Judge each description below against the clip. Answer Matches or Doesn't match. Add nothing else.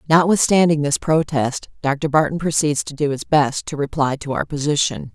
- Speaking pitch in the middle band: Matches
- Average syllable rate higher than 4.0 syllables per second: Matches